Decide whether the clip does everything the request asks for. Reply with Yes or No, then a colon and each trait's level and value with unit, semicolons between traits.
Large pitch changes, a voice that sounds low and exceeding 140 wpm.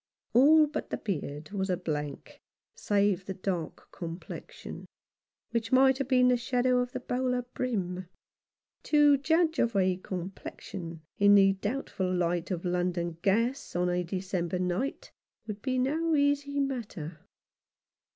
No: wide, 6.3 semitones; high, 200 Hz; average, 150 wpm